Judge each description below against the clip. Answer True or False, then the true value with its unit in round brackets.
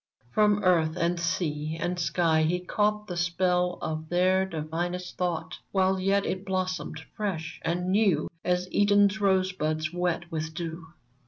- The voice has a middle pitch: True (180 Hz)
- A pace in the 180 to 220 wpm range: False (145 wpm)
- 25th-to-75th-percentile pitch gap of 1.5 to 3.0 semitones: True (2.5 semitones)